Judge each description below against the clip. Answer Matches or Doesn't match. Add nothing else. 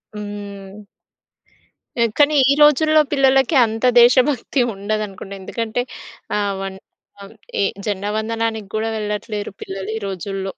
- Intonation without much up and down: Doesn't match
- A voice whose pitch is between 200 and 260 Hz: Matches